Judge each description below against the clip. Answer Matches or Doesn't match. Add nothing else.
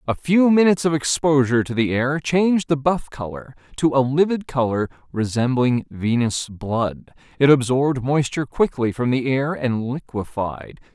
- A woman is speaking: Doesn't match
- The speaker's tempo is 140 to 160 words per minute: Matches